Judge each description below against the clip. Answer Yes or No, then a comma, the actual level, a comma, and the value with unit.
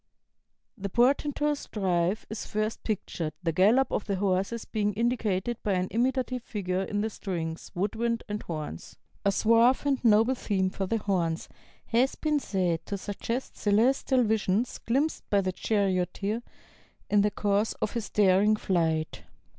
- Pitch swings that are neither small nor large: Yes, average, 3.8 semitones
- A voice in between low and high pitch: No, high, 210 Hz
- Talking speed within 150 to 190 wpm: Yes, average, 155 wpm